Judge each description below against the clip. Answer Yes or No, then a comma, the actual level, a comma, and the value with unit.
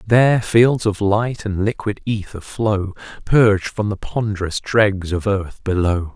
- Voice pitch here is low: Yes, low, 105 Hz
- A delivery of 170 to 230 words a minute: No, average, 155 wpm